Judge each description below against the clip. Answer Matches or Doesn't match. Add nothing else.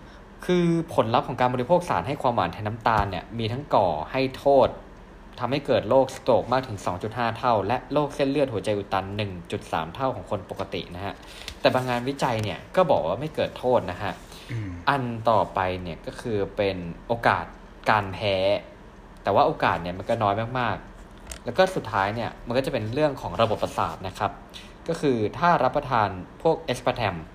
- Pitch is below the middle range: Matches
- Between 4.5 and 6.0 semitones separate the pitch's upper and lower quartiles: Matches